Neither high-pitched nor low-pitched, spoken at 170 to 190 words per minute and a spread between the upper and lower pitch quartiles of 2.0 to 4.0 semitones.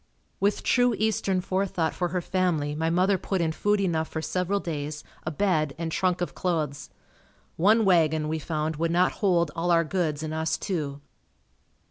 Yes: medium, 170 Hz; average, 175 wpm; average, 3.0 semitones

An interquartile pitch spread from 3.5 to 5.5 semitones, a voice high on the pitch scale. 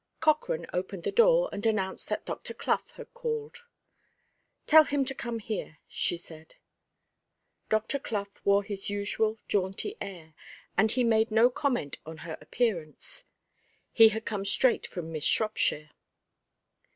Yes: average, 5.1 semitones; high, 215 Hz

